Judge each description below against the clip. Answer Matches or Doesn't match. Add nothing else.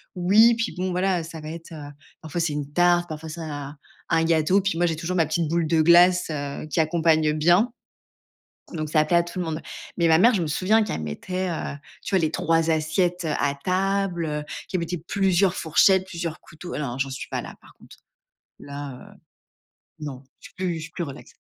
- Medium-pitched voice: Matches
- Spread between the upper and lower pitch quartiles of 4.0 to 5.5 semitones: Doesn't match